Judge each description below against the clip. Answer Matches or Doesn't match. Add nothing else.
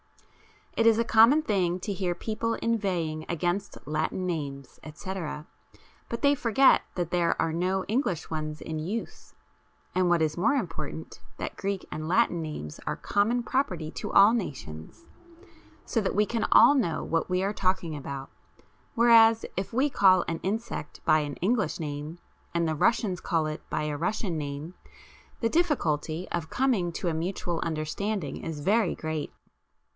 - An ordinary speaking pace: Matches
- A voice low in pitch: Doesn't match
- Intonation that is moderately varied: Doesn't match